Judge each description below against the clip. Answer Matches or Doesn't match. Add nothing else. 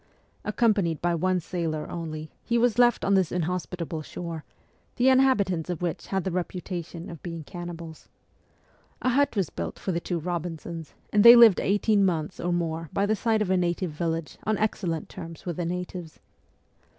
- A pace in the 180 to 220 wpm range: Matches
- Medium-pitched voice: Matches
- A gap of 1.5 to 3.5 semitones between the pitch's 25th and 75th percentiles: Matches